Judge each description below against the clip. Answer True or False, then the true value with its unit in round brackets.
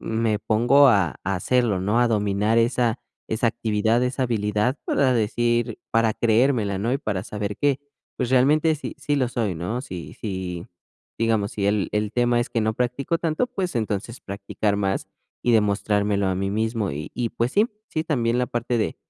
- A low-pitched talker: True (115 Hz)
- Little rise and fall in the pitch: False (3.2 semitones)